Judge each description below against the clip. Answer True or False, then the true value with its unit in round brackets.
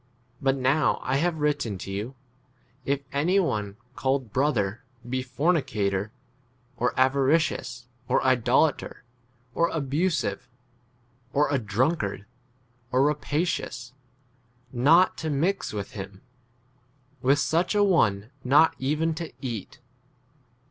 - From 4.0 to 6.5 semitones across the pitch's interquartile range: True (4.7 semitones)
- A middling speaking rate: False (115 wpm)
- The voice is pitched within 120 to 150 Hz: True (135 Hz)